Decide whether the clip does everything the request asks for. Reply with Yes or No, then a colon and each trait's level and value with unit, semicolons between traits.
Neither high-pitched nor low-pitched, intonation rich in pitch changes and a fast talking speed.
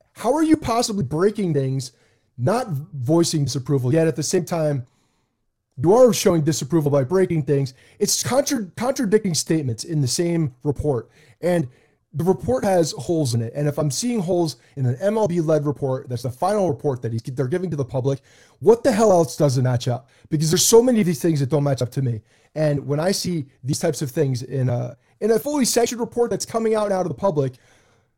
Yes: medium, 150 Hz; wide, 5.8 semitones; fast, 215 wpm